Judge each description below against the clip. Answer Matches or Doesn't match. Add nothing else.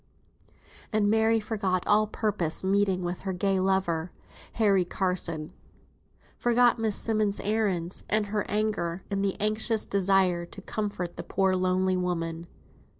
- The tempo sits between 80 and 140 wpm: Matches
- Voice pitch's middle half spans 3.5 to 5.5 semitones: Doesn't match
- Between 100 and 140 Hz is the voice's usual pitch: Doesn't match